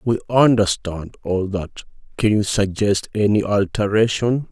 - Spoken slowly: Yes, slow, 120 wpm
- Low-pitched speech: Yes, low, 105 Hz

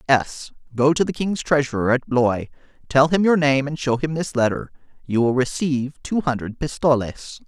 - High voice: No, medium, 140 Hz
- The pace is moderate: Yes, average, 175 wpm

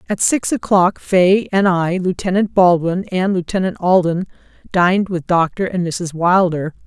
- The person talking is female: Yes, female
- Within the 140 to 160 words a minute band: Yes, average, 150 wpm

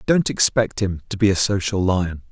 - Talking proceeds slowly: No, fast, 205 wpm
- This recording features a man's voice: Yes, male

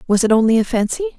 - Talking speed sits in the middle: No, fast, 255 wpm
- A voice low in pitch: No, high, 245 Hz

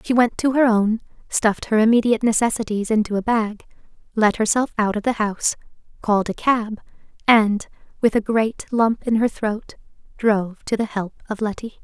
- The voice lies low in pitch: No, high, 220 Hz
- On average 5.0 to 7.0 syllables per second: Yes, 5.4 syllables/s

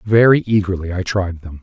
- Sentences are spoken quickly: No, average, 185 wpm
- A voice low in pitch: Yes, very low, 95 Hz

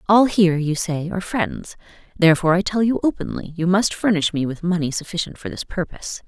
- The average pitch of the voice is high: No, medium, 175 Hz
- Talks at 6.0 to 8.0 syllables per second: Yes, 6.1 syllables/s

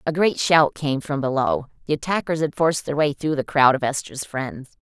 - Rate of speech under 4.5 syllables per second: No, 5.2 syllables/s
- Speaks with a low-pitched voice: No, medium, 145 Hz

